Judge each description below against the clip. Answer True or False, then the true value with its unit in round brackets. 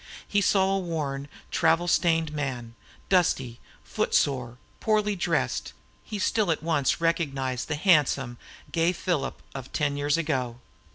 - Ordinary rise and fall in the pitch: True (4.4 semitones)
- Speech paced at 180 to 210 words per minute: False (135 wpm)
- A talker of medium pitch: True (160 Hz)